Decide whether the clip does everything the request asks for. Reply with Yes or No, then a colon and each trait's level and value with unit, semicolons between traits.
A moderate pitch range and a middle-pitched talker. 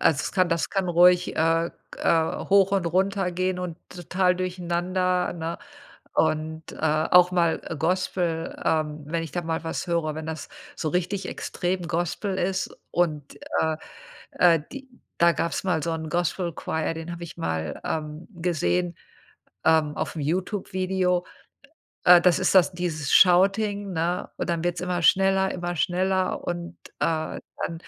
No: narrow, 2.2 semitones; medium, 175 Hz